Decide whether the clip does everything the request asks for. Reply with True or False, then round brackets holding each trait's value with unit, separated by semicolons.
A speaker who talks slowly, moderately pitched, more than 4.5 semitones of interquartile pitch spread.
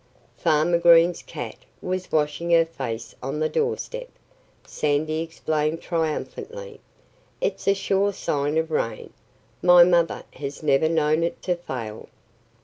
False (130 wpm; 165 Hz; 2.9 semitones)